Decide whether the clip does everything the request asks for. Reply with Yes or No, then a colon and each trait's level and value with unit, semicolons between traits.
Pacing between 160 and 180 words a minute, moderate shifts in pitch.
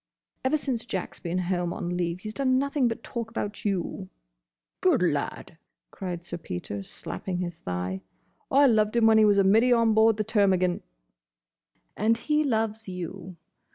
Yes: average, 165 wpm; average, 4.4 semitones